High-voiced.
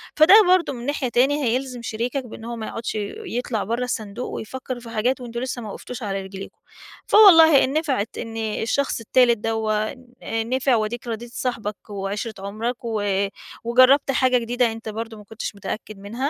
Yes: high, 235 Hz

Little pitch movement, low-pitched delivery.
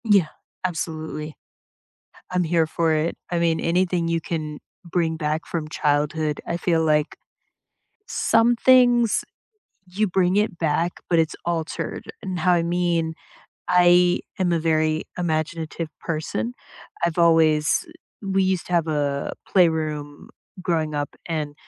No: narrow, 2.2 semitones; medium, 165 Hz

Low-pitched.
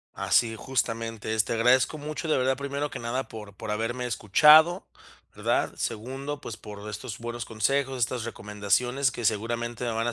Yes: low, 120 Hz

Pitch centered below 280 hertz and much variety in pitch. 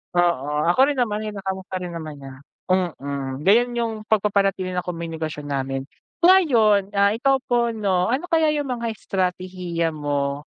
Yes: medium, 185 Hz; wide, 5.7 semitones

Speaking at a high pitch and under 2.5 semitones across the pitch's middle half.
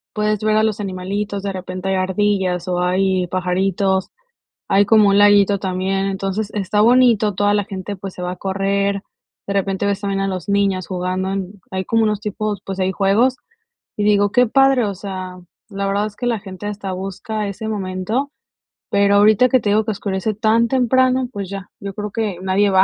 Yes: high, 200 Hz; narrow, 1.9 semitones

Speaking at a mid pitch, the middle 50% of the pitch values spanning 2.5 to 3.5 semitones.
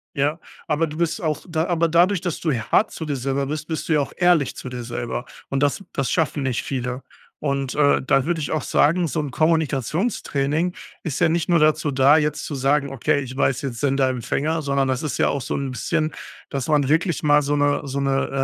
Yes: medium, 145 Hz; average, 2.8 semitones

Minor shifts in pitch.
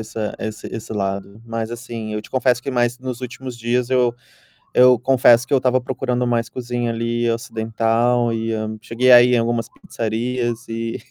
Yes: narrow, 1.6 semitones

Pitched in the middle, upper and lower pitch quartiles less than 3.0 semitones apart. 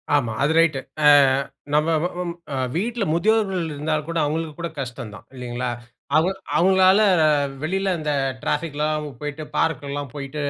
No: medium, 155 Hz; average, 4.0 semitones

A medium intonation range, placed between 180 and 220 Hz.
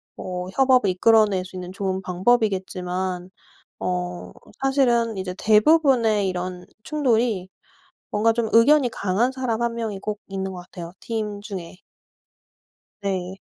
Yes: average, 4.0 semitones; high, 205 Hz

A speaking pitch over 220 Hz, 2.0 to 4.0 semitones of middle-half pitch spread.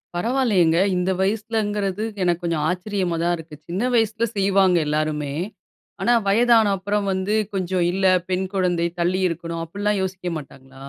No: medium, 185 Hz; average, 3.3 semitones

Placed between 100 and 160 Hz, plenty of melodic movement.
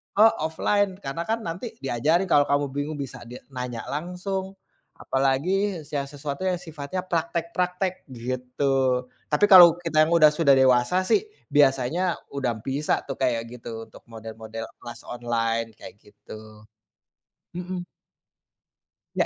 Yes: medium, 140 Hz; wide, 6.2 semitones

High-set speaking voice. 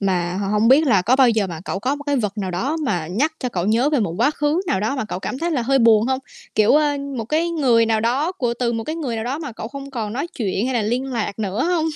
Yes: high, 240 Hz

